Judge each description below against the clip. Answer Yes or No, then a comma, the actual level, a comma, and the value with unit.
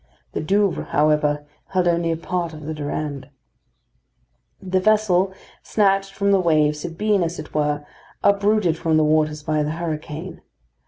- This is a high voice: No, medium, 165 Hz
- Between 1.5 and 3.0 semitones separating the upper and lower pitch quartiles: No, average, 3.9 semitones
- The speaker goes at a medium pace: Yes, average, 155 wpm